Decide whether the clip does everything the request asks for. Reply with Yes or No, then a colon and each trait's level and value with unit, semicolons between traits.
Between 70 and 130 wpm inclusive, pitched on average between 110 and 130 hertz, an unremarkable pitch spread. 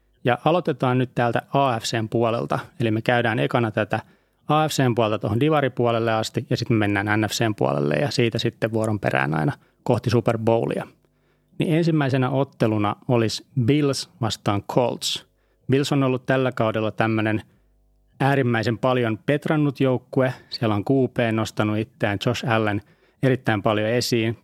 No: average, 140 wpm; low, 120 Hz; average, 3.2 semitones